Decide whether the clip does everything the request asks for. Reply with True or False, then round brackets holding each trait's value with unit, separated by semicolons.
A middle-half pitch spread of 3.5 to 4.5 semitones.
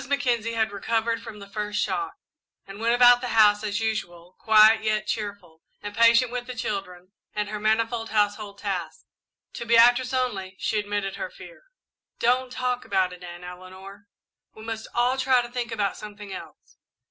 False (3.0 semitones)